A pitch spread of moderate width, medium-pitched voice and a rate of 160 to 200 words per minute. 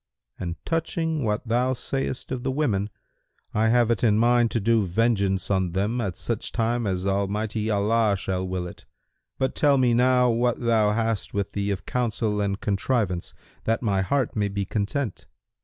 No: average, 3.5 semitones; low, 110 Hz; average, 175 wpm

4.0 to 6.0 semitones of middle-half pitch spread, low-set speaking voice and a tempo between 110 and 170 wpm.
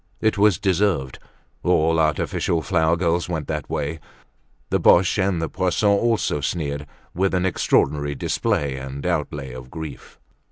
Yes: average, 4.4 semitones; very low, 80 Hz; average, 145 wpm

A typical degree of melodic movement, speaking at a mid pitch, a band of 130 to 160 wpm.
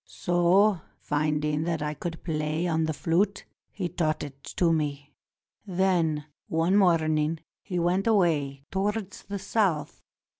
Yes: average, 3.5 semitones; medium, 165 Hz; slow, 135 wpm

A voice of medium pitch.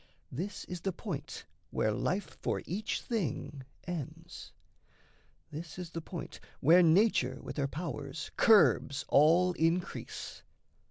Yes: medium, 170 Hz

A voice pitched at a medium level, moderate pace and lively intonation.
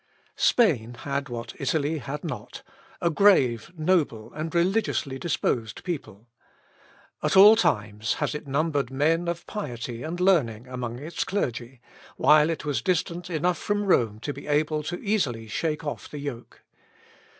Yes: medium, 150 Hz; average, 150 wpm; wide, 5.8 semitones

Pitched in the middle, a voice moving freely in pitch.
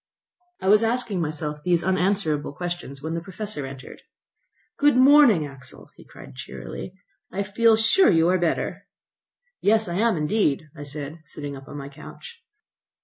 Yes: medium, 175 Hz; wide, 6.3 semitones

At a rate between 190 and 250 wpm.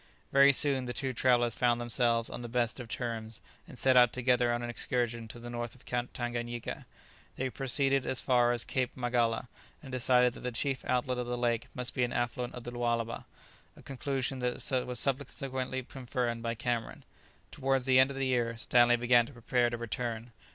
Yes: average, 195 wpm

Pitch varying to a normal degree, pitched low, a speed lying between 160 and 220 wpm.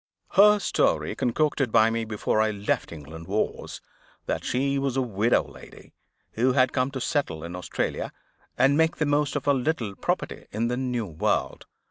Yes: average, 4.5 semitones; low, 125 Hz; average, 175 wpm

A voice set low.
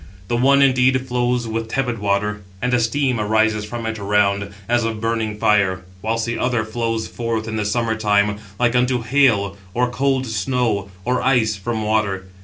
Yes: low, 115 Hz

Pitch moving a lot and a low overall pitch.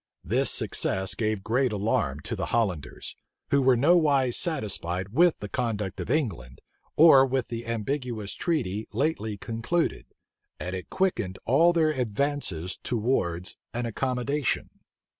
Yes: wide, 5.8 semitones; low, 115 Hz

